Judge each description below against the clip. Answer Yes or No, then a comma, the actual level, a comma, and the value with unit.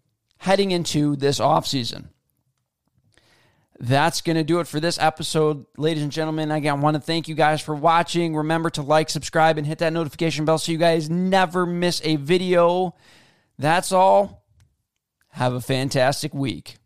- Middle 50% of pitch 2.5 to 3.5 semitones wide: Yes, average, 3.0 semitones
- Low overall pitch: No, medium, 155 Hz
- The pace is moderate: Yes, average, 165 wpm